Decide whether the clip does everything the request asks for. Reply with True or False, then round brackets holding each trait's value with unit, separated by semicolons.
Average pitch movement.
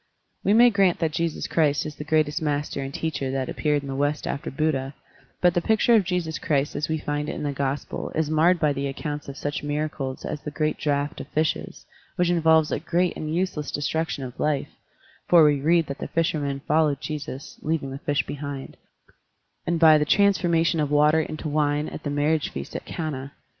False (2.1 semitones)